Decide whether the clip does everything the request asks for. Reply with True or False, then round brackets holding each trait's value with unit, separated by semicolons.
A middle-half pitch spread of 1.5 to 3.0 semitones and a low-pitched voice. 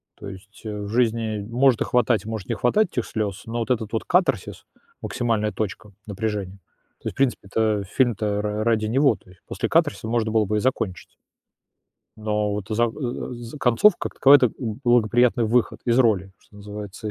True (2.4 semitones; 110 Hz)